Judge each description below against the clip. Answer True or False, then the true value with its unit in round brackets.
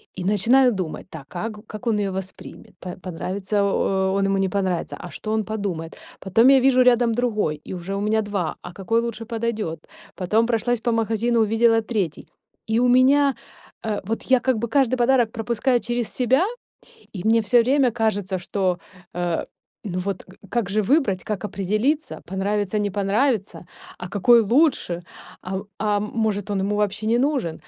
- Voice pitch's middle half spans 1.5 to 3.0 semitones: False (3.6 semitones)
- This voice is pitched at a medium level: False (215 Hz)